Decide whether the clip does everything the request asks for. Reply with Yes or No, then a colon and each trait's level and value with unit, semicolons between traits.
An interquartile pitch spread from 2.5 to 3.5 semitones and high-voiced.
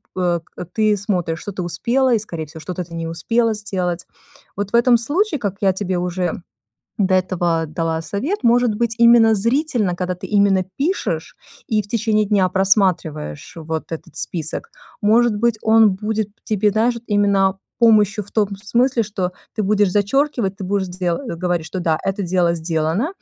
No: average, 3.9 semitones; high, 200 Hz